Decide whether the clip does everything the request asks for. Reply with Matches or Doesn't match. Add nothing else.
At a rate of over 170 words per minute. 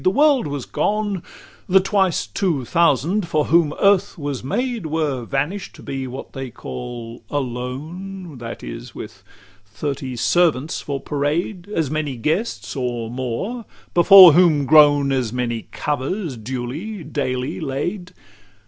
Doesn't match